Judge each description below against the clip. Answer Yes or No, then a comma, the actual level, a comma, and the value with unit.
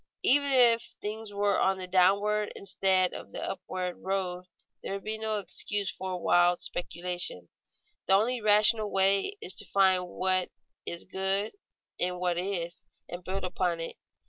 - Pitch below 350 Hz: Yes, high, 190 Hz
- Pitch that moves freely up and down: No, narrow, 2.4 semitones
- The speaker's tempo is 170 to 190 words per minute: No, average, 160 wpm